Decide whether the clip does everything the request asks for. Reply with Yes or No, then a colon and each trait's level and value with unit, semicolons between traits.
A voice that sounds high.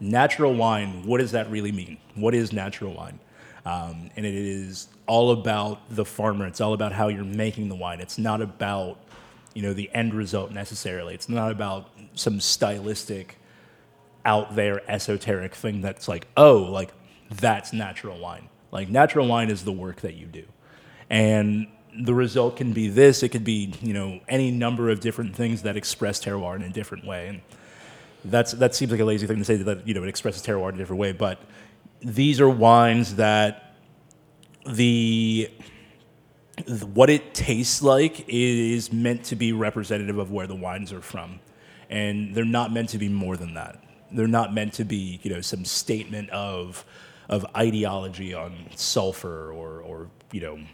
No: low, 105 Hz